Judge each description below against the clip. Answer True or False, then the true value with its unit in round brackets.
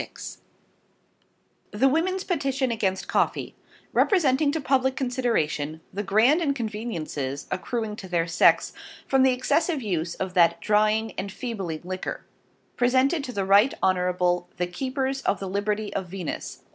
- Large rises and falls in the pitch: True (6.3 semitones)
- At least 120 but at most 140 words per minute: True (135 wpm)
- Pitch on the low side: False (215 Hz)